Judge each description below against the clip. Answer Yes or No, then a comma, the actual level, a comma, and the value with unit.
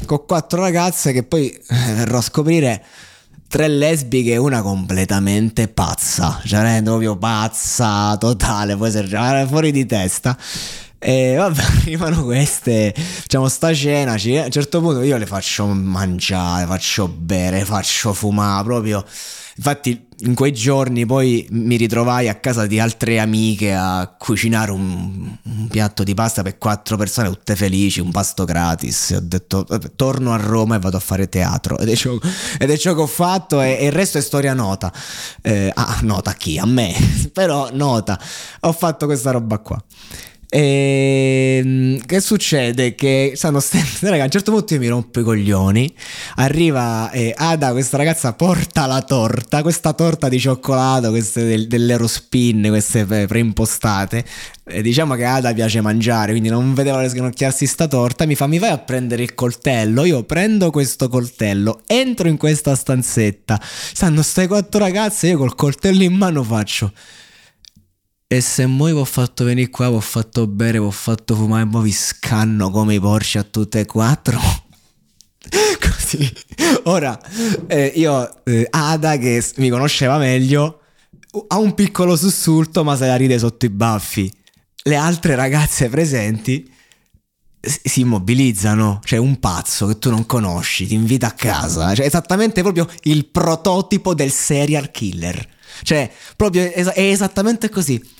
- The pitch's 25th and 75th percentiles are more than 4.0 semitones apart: Yes, wide, 5.4 semitones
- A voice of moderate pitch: No, low, 125 Hz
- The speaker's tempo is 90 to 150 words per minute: No, average, 160 wpm